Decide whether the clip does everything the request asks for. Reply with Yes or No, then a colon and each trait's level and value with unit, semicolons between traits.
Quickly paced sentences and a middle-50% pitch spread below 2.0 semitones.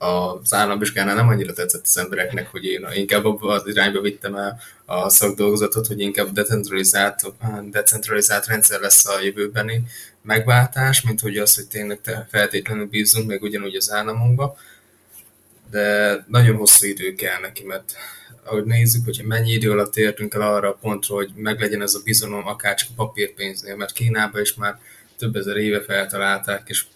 Yes: fast, 160 wpm; narrow, 1.5 semitones